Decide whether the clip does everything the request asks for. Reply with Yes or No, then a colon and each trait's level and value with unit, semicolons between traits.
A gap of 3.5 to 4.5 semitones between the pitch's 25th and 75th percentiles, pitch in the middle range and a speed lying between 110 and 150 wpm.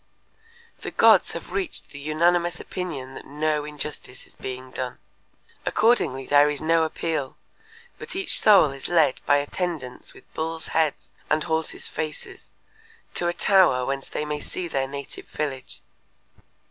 Yes: average, 3.9 semitones; medium, 150 Hz; average, 145 wpm